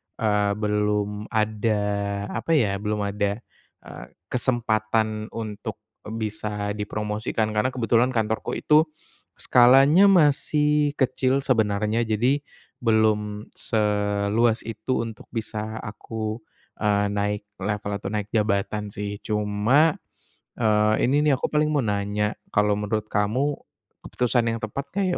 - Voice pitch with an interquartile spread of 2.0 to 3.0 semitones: Yes, average, 2.7 semitones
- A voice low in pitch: Yes, low, 110 Hz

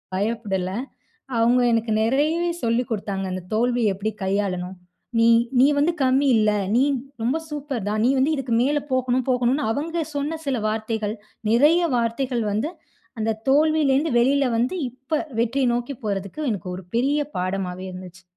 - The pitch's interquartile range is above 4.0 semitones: Yes, average, 4.7 semitones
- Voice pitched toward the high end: Yes, high, 240 Hz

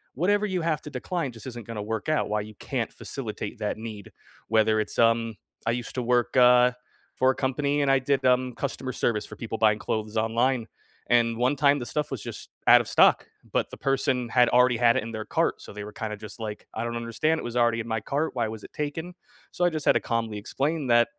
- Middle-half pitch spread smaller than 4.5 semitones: Yes, average, 3.3 semitones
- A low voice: Yes, low, 120 Hz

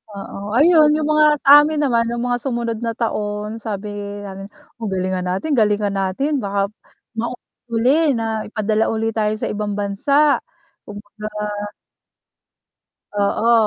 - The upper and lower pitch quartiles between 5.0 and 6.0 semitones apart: No, average, 3.3 semitones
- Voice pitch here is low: No, high, 225 Hz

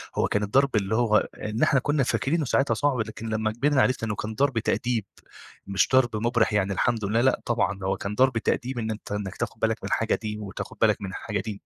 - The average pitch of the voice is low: Yes, low, 110 Hz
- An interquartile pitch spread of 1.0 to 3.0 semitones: No, average, 3.4 semitones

